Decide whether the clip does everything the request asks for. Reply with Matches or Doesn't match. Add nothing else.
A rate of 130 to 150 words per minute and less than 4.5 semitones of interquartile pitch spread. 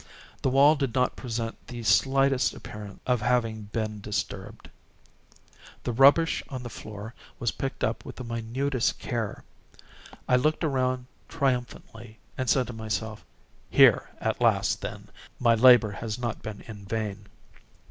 Matches